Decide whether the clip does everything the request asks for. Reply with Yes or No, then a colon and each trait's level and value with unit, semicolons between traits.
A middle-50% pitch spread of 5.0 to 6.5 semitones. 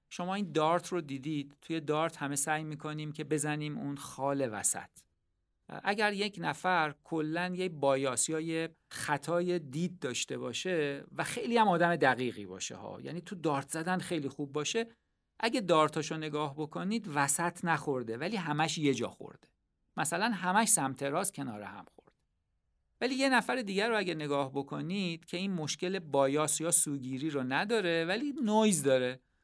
No: average, 4.2 semitones